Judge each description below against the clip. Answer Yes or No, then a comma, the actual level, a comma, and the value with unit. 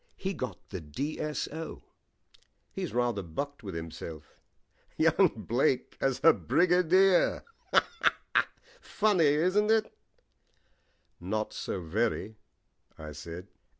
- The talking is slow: Yes, slow, 95 wpm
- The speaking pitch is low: Yes, low, 125 Hz